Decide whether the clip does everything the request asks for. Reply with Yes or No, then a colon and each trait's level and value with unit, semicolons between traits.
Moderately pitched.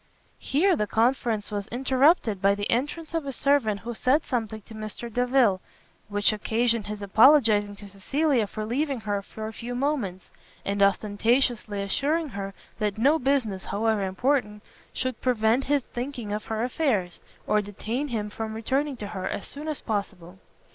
No: high, 225 Hz